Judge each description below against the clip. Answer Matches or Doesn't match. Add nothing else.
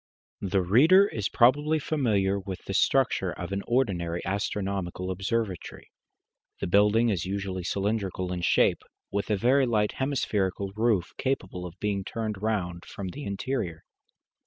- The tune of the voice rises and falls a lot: Doesn't match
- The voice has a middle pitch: Doesn't match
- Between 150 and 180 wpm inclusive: Doesn't match